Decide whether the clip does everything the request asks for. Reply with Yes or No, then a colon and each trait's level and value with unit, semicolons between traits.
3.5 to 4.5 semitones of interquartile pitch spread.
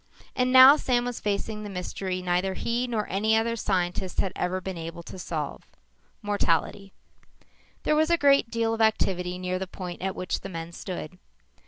Yes: average, 4.1 semitones